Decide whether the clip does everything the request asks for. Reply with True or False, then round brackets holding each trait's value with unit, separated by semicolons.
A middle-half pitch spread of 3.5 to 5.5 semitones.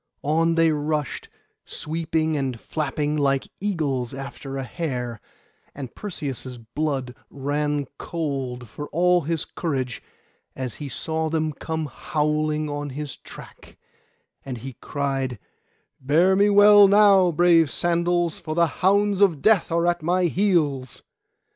True (3.9 semitones)